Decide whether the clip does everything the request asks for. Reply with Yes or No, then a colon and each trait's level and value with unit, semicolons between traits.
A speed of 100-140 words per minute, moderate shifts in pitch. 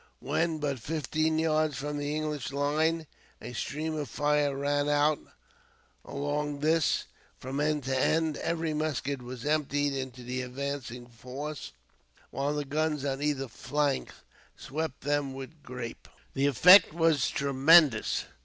No: slow, 135 wpm; narrow, 2.3 semitones